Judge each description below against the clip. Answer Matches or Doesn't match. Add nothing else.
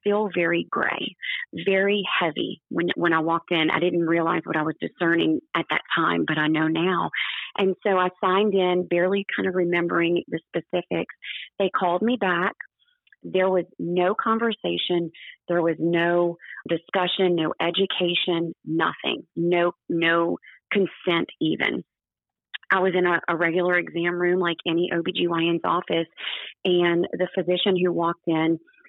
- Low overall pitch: Doesn't match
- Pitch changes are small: Matches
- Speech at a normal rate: Matches